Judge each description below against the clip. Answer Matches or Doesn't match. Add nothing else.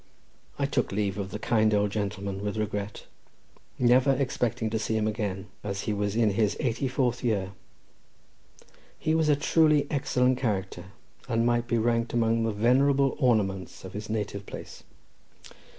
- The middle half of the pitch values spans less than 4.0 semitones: Matches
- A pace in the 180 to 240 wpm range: Doesn't match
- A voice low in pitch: Matches